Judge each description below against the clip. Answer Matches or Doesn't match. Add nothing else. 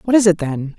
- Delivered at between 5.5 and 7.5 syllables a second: Doesn't match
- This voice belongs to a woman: Matches